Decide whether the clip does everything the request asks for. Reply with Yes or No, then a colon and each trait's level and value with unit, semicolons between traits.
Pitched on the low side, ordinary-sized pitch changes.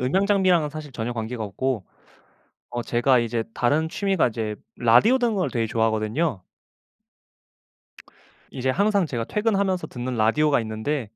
No: low, 130 Hz; wide, 7.7 semitones